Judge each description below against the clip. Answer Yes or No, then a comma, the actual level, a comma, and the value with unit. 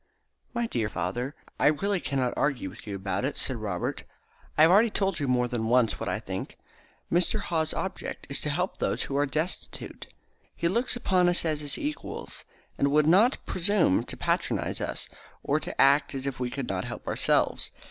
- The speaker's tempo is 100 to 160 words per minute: No, average, 195 wpm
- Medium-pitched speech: Yes, medium, 145 Hz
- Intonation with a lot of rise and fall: Yes, wide, 6.3 semitones